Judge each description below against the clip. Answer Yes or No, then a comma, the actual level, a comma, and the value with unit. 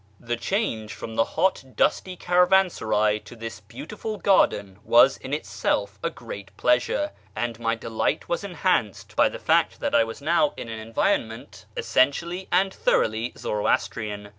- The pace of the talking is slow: No, average, 150 wpm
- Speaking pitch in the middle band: No, low, 115 Hz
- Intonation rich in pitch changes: Yes, wide, 8.5 semitones